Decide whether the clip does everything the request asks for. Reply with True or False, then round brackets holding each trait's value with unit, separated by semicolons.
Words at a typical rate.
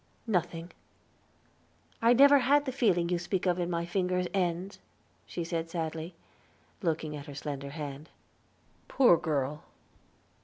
False (130 wpm)